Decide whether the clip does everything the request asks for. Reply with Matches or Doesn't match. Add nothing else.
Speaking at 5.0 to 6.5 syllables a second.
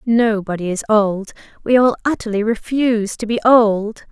Doesn't match